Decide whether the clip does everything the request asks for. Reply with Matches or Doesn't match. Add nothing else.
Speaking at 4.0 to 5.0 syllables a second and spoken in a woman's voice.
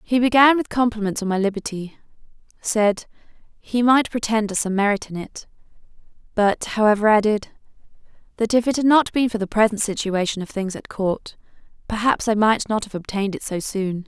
Doesn't match